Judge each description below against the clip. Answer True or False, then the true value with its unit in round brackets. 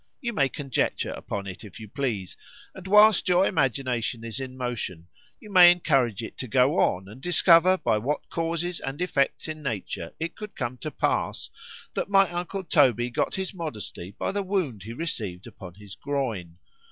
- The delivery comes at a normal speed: True (175 wpm)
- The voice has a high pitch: False (135 Hz)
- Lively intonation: True (8.0 semitones)